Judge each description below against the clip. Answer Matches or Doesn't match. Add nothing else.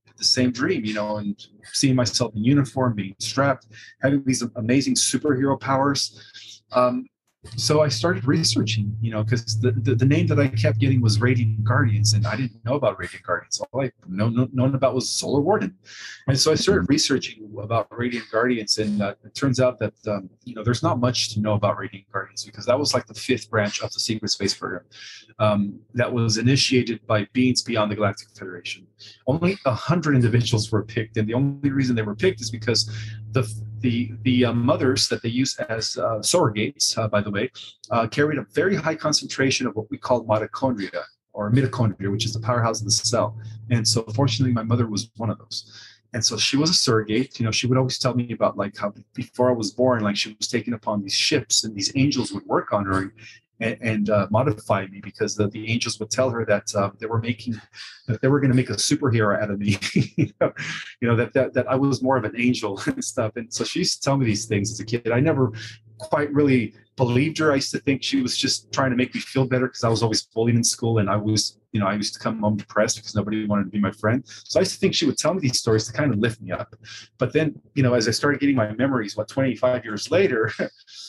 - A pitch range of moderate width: Matches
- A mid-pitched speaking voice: Doesn't match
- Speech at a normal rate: Doesn't match